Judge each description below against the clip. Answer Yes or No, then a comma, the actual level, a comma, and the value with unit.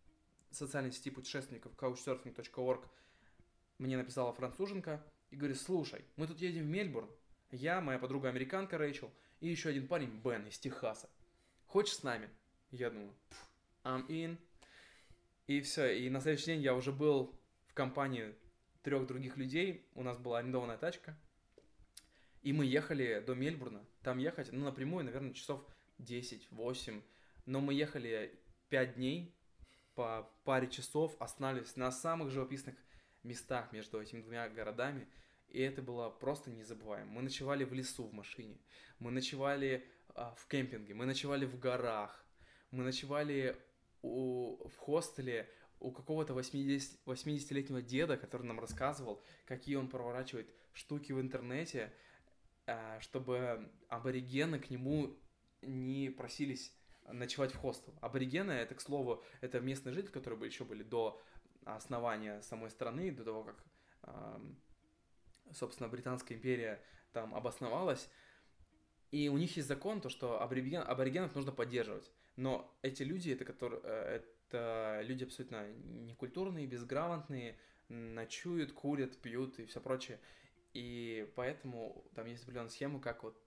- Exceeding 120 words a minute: Yes, average, 135 wpm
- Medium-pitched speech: No, low, 130 Hz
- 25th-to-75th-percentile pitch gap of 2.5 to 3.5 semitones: Yes, average, 2.9 semitones